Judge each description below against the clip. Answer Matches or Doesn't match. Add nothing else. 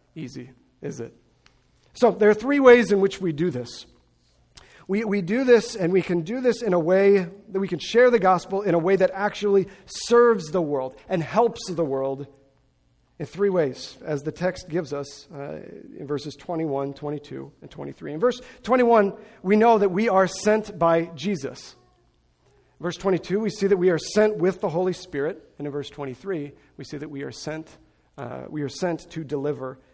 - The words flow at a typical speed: Matches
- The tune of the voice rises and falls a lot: Matches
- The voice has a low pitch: Doesn't match